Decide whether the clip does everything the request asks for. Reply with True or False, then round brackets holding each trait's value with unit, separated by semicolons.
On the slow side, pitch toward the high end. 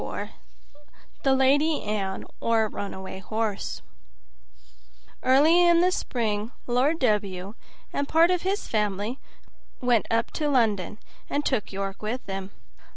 True (130 wpm; 230 Hz)